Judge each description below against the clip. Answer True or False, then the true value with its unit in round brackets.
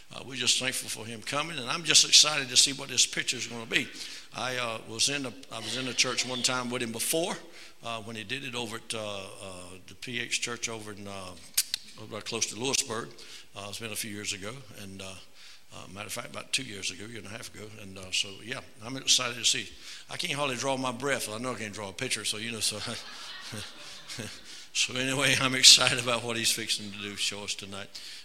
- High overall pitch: False (115 Hz)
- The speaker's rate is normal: False (245 wpm)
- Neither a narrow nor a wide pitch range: True (3.7 semitones)